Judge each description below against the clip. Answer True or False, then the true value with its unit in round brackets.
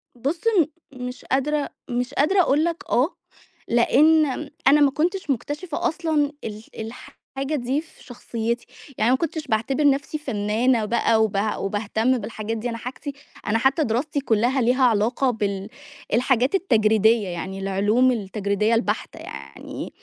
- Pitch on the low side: False (245 Hz)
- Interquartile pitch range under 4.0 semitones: False (4.7 semitones)